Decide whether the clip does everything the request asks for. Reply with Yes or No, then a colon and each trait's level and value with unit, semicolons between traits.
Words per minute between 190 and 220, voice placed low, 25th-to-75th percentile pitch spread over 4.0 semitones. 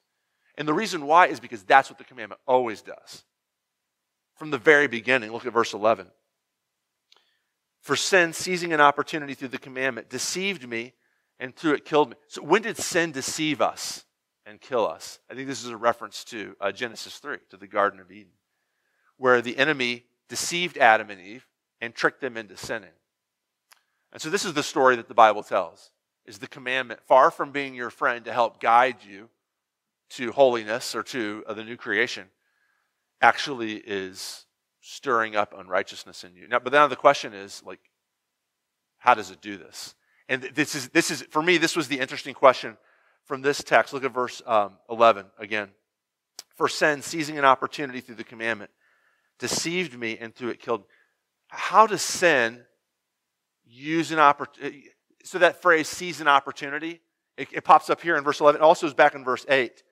No: average, 180 wpm; low, 130 Hz; average, 4.7 semitones